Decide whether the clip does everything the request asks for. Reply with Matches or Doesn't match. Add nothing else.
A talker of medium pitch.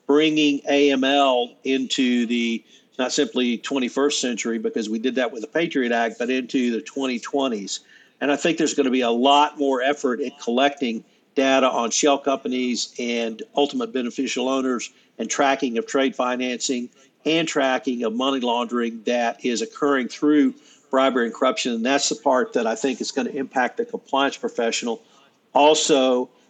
Doesn't match